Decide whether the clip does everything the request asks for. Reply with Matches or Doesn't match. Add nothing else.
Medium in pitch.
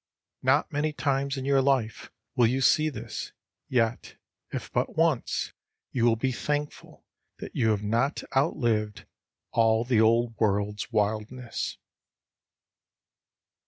Doesn't match